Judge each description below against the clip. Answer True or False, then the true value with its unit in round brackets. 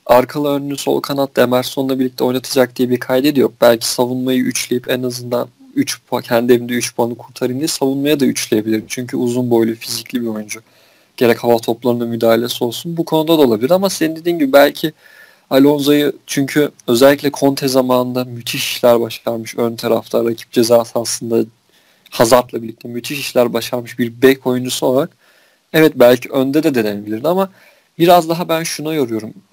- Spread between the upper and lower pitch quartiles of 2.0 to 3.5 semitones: True (3.2 semitones)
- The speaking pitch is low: True (125 Hz)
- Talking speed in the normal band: False (160 wpm)